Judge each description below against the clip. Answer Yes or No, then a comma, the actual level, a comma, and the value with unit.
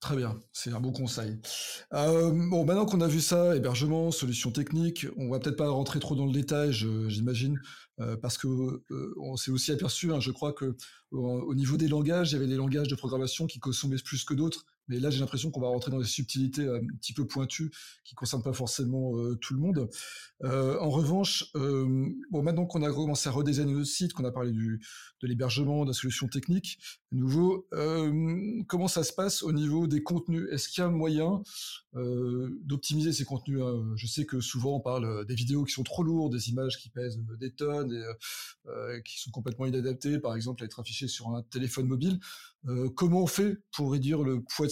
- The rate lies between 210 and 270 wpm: Yes, average, 215 wpm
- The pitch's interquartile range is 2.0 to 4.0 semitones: Yes, average, 3.7 semitones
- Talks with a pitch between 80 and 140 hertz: Yes, low, 135 Hz